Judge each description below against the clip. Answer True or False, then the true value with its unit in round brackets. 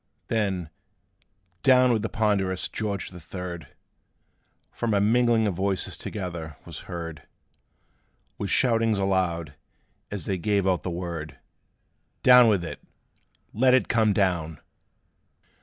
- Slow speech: True (125 wpm)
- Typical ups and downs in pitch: True (4.2 semitones)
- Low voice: True (95 Hz)